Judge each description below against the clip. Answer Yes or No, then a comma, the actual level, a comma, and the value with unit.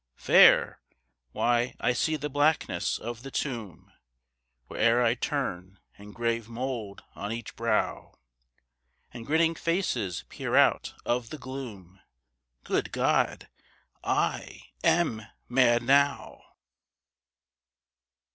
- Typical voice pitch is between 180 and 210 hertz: No, low, 120 Hz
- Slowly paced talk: Yes, slow, 105 wpm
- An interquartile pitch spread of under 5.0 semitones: Yes, average, 3.8 semitones